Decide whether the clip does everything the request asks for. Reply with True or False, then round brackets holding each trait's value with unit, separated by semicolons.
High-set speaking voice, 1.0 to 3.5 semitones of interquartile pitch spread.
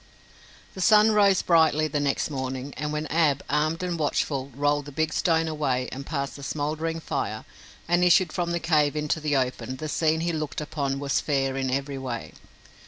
False (150 Hz; 2.8 semitones)